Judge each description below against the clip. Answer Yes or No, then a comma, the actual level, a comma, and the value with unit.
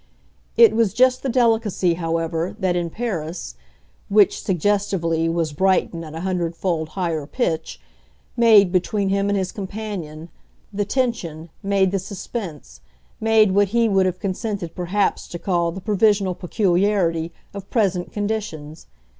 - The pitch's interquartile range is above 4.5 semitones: No, average, 3.7 semitones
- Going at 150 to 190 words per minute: No, average, 140 wpm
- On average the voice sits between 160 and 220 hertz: Yes, high, 190 Hz